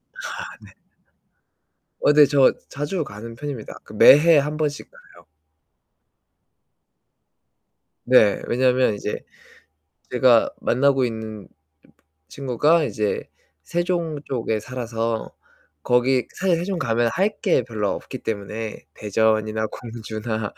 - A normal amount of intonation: Yes, average, 4.9 semitones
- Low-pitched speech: Yes, low, 125 Hz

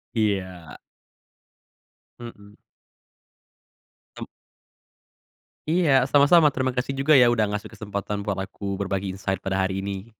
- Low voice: Yes, low, 105 Hz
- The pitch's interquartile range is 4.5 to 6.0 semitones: Yes, average, 4.9 semitones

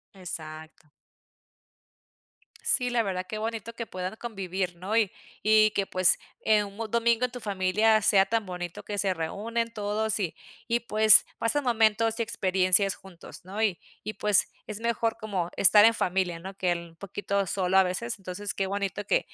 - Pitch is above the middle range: Yes, high, 205 Hz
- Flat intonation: No, average, 3.1 semitones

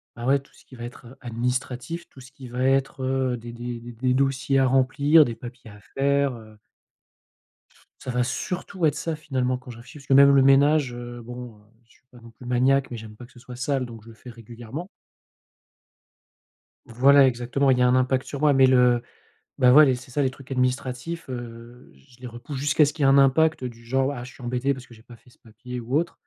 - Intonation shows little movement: Yes, narrow, 2.2 semitones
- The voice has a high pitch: No, low, 125 Hz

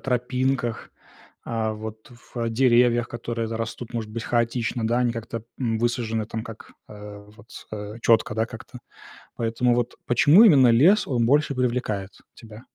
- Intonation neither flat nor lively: No, narrow, 1.9 semitones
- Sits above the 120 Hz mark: No, low, 115 Hz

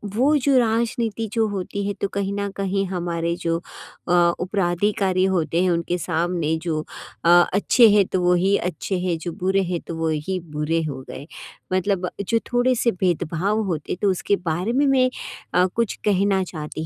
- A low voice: No, medium, 185 Hz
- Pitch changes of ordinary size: Yes, average, 3.2 semitones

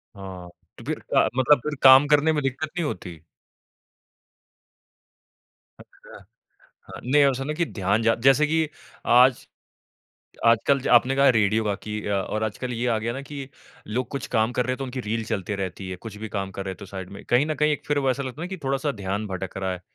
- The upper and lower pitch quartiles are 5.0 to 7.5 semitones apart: Yes, average, 5.3 semitones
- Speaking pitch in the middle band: No, low, 120 Hz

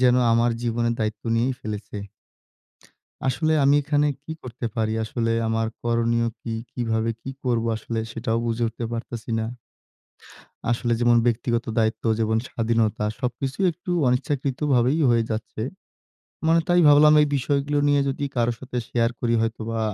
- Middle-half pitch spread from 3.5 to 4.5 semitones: No, average, 2.7 semitones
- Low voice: Yes, low, 120 Hz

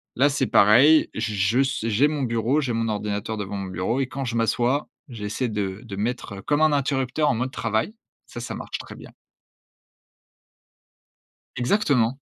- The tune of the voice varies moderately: Yes, average, 4.2 semitones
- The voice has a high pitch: No, low, 120 Hz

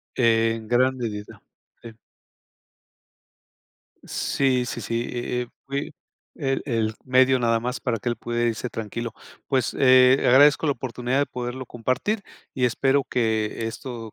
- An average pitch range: No, narrow, 2.2 semitones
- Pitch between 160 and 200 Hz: No, low, 125 Hz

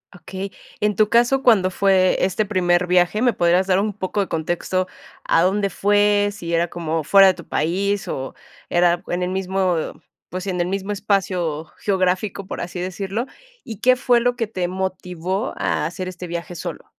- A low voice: No, medium, 185 Hz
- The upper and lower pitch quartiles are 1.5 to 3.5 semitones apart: Yes, narrow, 2.4 semitones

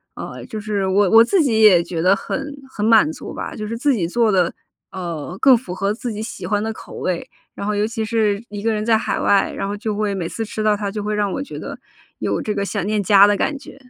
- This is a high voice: Yes, high, 210 Hz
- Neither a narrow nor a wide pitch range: No, narrow, 2.1 semitones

